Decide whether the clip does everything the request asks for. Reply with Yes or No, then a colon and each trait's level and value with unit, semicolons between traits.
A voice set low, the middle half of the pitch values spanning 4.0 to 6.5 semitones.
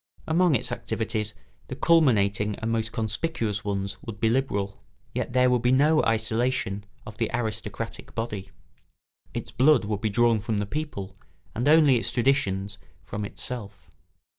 No: low, 110 Hz; average, 3.5 semitones